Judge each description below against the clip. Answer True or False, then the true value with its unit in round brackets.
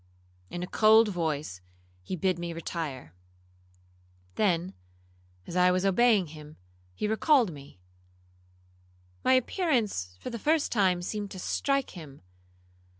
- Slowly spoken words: True (120 wpm)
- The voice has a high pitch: False (175 Hz)